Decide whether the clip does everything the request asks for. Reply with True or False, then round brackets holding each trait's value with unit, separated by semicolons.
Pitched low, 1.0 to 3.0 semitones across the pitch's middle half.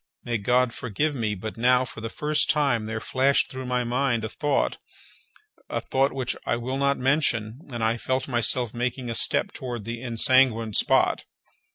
True (125 Hz; 2.4 semitones)